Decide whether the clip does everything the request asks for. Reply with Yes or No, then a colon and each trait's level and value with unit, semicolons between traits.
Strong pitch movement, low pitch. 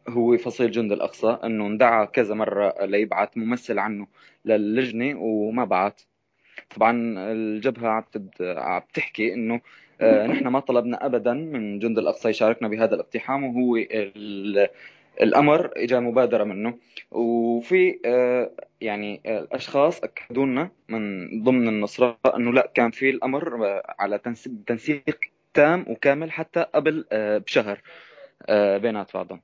No: average, 2.7 semitones; low, 115 Hz